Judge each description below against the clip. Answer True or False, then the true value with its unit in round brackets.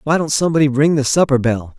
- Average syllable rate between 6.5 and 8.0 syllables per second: True (6.6 syllables/s)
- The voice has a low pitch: False (145 Hz)